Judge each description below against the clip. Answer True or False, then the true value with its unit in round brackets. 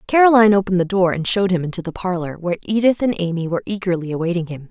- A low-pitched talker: False (185 Hz)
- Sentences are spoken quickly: True (230 wpm)